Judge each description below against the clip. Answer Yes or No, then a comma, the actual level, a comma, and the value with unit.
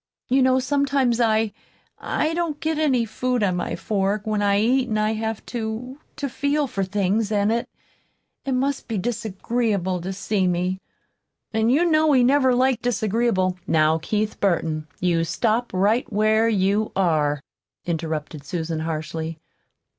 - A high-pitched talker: Yes, high, 215 Hz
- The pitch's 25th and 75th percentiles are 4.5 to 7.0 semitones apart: Yes, average, 5.1 semitones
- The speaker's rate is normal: Yes, average, 155 wpm